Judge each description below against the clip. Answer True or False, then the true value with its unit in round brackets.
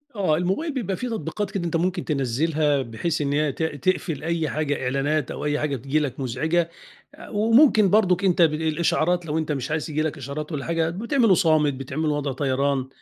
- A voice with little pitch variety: False (3.7 semitones)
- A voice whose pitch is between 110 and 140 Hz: False (155 Hz)